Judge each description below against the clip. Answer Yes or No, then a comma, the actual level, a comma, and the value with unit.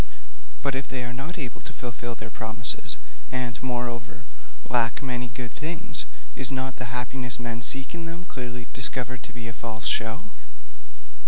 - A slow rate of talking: No, average, 165 wpm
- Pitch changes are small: Yes, narrow, 2.0 semitones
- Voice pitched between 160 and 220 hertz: No, low, 125 Hz